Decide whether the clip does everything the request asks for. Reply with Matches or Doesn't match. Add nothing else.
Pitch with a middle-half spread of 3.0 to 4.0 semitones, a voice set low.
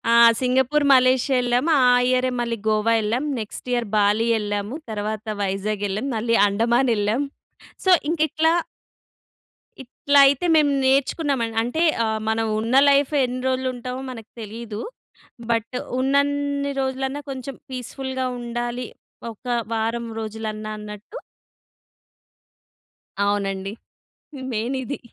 Doesn't match